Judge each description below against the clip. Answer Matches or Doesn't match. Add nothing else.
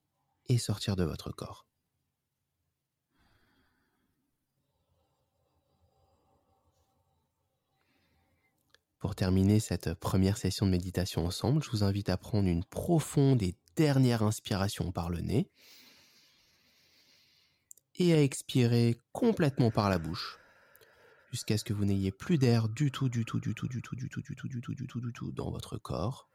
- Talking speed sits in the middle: Doesn't match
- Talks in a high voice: Doesn't match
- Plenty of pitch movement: Matches